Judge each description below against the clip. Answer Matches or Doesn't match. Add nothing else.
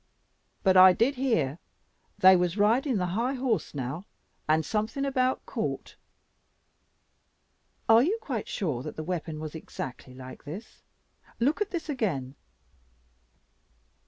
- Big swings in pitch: Matches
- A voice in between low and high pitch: Doesn't match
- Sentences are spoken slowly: Matches